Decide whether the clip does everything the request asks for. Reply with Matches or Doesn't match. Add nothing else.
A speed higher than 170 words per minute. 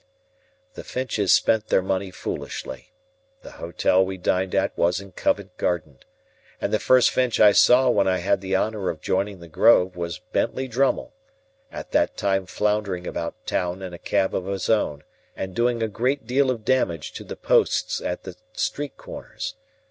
Matches